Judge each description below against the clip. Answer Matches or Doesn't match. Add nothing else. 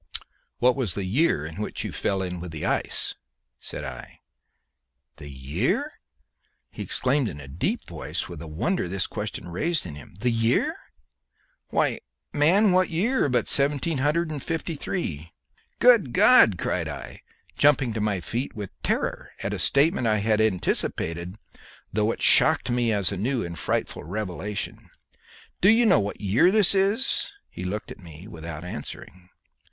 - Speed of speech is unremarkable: Matches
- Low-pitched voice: Matches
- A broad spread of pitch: Matches